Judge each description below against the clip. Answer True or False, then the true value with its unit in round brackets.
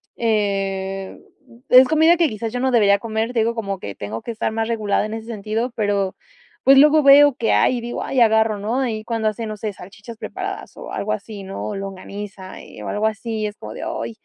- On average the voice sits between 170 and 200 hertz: False (220 Hz)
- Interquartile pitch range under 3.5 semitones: True (2.9 semitones)